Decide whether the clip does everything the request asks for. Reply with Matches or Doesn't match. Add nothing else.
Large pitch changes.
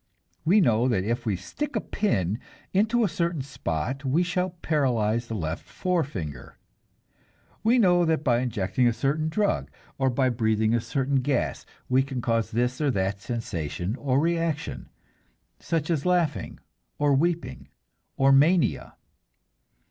Matches